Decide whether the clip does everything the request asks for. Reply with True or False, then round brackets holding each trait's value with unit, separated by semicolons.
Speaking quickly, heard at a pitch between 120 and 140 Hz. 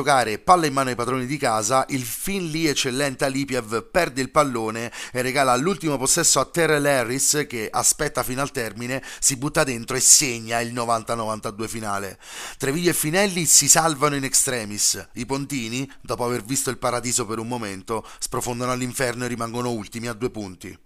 True (175 wpm; 130 Hz)